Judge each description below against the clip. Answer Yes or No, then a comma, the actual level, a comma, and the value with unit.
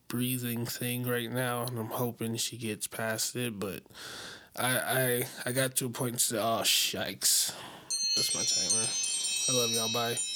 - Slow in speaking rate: No, average, 175 wpm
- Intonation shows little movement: Yes, narrow, 1.4 semitones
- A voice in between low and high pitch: No, low, 120 Hz